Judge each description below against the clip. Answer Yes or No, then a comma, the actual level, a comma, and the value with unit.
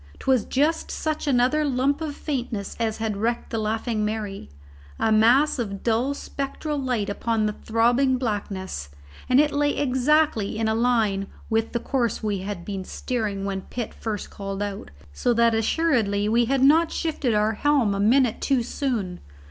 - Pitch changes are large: No, average, 4.4 semitones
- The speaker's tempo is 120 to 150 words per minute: No, average, 170 wpm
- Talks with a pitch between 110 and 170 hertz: No, high, 230 Hz